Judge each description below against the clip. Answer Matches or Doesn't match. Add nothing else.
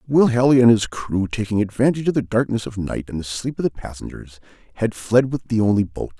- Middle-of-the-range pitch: Doesn't match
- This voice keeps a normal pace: Doesn't match